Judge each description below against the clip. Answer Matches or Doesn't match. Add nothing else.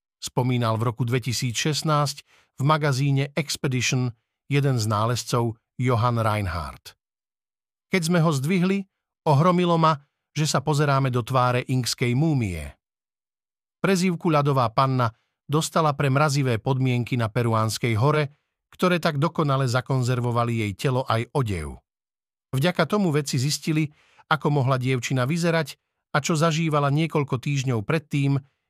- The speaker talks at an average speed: Matches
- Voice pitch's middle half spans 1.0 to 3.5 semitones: Doesn't match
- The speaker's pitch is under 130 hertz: Doesn't match